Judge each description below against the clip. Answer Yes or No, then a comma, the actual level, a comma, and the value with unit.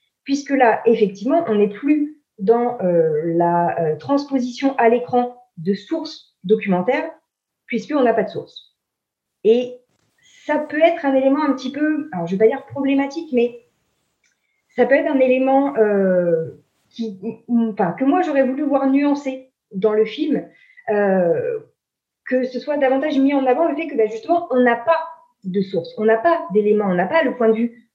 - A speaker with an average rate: Yes, average, 180 wpm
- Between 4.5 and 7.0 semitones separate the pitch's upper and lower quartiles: Yes, average, 5.1 semitones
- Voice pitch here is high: Yes, very high, 250 Hz